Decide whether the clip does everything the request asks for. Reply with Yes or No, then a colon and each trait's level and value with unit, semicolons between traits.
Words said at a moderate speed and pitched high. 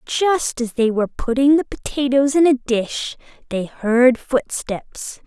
Yes: average, 150 wpm; very high, 255 Hz